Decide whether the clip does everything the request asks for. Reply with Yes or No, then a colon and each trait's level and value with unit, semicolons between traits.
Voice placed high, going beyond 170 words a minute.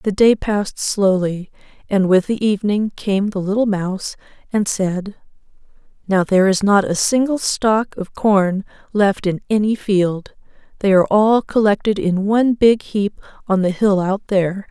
No: high, 200 Hz; average, 165 wpm